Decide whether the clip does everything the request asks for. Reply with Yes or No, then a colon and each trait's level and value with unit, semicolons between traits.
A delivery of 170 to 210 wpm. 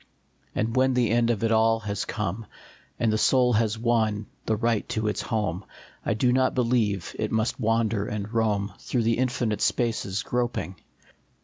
Yes: average, 175 wpm